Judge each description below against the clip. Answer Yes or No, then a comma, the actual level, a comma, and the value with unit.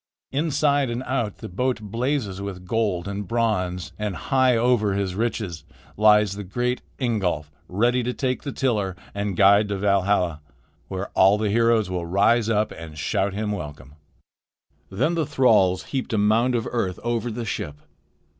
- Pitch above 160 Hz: No, low, 105 Hz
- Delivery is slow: No, average, 165 wpm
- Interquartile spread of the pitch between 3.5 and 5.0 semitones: Yes, average, 3.9 semitones